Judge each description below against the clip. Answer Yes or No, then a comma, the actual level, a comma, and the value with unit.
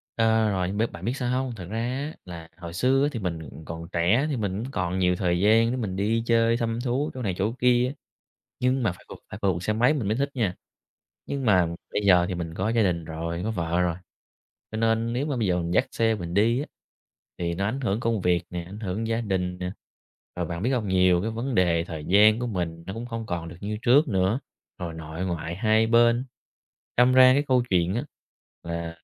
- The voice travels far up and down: No, average, 4.9 semitones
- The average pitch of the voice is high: No, low, 105 Hz